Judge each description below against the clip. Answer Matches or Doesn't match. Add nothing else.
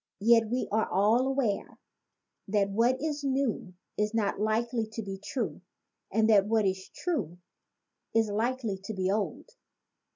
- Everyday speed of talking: Matches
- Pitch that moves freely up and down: Doesn't match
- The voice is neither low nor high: Doesn't match